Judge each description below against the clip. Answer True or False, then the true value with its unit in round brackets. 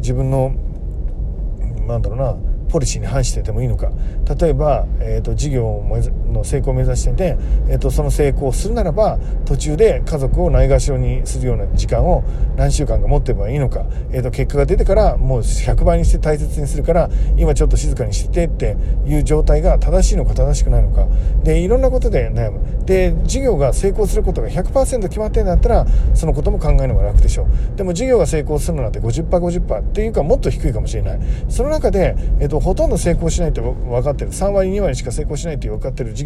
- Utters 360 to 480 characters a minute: True (420 characters per minute)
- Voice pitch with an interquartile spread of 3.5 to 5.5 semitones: True (5.2 semitones)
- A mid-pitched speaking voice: False (130 Hz)